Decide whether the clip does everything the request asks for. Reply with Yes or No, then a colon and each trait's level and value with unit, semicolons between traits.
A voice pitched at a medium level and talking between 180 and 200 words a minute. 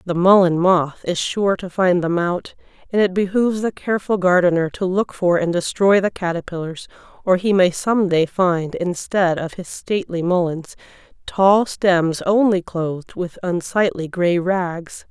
No: medium, 180 Hz; average, 165 wpm